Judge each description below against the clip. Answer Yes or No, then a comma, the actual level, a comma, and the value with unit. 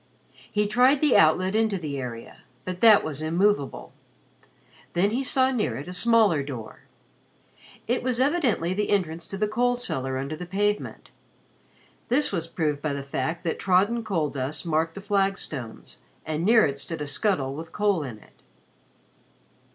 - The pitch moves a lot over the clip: Yes, wide, 6.1 semitones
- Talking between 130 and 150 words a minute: No, average, 165 wpm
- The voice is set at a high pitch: No, medium, 180 Hz